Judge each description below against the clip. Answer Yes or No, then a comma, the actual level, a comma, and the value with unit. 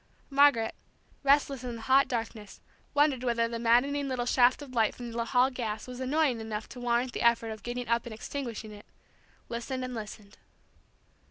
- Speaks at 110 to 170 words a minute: No, average, 180 wpm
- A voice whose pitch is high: Yes, high, 240 Hz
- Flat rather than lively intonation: Yes, narrow, 2.3 semitones